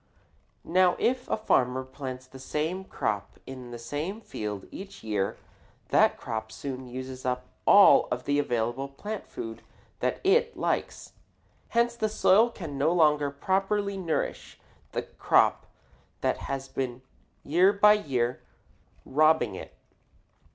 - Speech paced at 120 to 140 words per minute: Yes, slow, 135 wpm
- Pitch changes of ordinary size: No, wide, 7.3 semitones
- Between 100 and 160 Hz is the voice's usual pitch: Yes, medium, 140 Hz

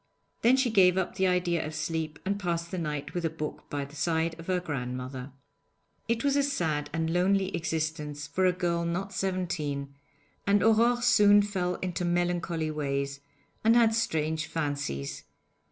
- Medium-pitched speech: Yes, medium, 170 Hz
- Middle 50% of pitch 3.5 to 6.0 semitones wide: Yes, average, 3.9 semitones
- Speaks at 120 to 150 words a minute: No, average, 170 wpm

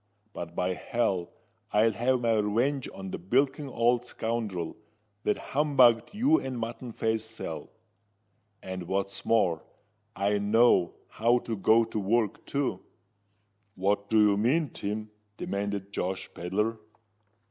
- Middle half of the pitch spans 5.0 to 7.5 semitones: No, average, 3.3 semitones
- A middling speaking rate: No, slow, 130 wpm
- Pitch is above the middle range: No, low, 110 Hz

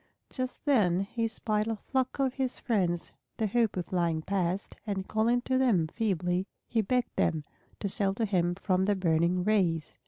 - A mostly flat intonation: No, average, 4.4 semitones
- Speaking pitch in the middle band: No, high, 200 Hz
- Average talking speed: Yes, average, 165 wpm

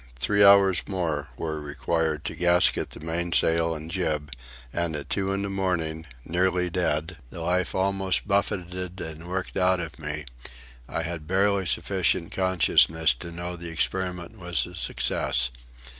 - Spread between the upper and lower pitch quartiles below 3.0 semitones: Yes, narrow, 2.6 semitones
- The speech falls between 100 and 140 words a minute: No, average, 150 wpm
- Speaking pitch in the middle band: No, very low, 85 Hz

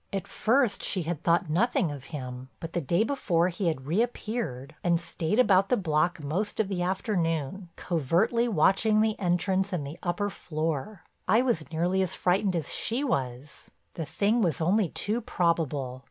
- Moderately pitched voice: Yes, medium, 175 Hz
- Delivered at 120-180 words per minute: Yes, average, 170 wpm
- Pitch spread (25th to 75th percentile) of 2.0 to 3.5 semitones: No, average, 4.6 semitones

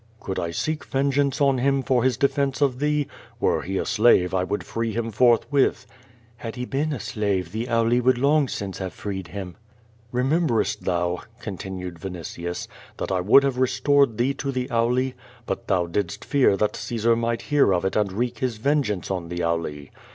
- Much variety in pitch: Yes, wide, 5.9 semitones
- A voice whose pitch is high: No, low, 115 Hz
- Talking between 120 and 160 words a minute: No, average, 190 wpm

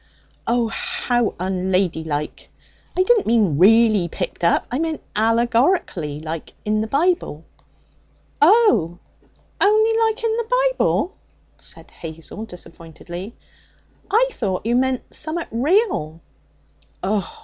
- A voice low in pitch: No, high, 225 Hz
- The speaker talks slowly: Yes, slow, 110 wpm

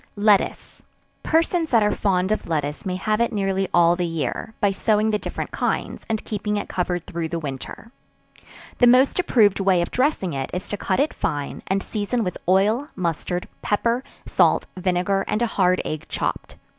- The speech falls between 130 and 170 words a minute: No, average, 180 wpm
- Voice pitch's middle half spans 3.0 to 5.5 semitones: Yes, average, 3.6 semitones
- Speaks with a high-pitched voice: Yes, high, 195 Hz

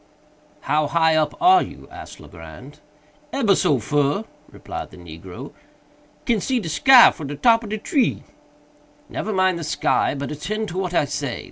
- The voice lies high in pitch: No, medium, 170 Hz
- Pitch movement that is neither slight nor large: No, wide, 6.9 semitones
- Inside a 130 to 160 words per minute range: No, average, 170 wpm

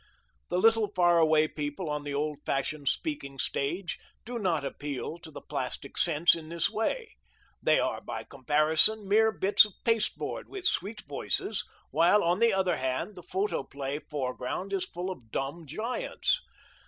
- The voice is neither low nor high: Yes, medium, 170 Hz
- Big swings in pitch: Yes, wide, 6.0 semitones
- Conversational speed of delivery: Yes, average, 160 wpm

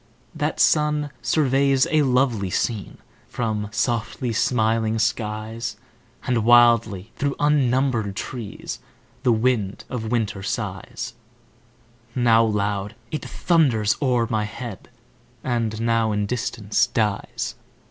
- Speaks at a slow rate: Yes, slow, 105 wpm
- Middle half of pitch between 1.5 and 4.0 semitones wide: Yes, average, 2.9 semitones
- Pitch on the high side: No, low, 115 Hz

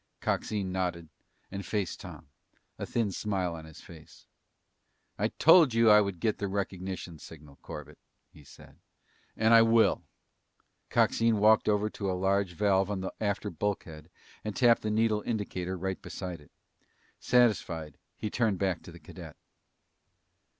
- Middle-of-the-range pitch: No, low, 100 Hz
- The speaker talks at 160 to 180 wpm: No, average, 150 wpm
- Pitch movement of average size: Yes, average, 3.3 semitones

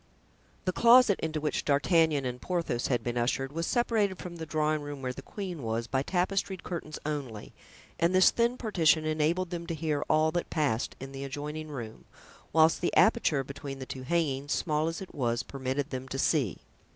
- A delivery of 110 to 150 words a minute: No, average, 190 wpm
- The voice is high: No, medium, 155 Hz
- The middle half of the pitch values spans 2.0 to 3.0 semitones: No, average, 4.2 semitones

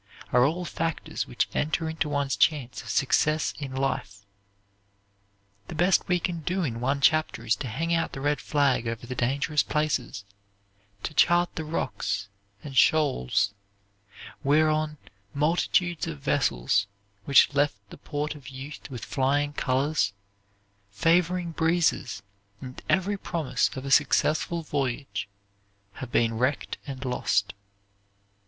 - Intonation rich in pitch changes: No, average, 4.1 semitones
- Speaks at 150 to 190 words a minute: No, slow, 135 wpm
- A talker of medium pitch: Yes, medium, 145 Hz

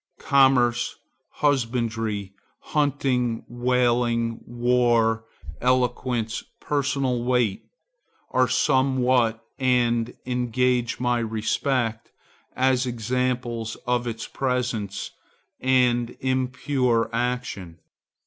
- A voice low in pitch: Yes, low, 125 Hz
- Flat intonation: Yes, narrow, 1.7 semitones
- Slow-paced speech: Yes, slow, 70 wpm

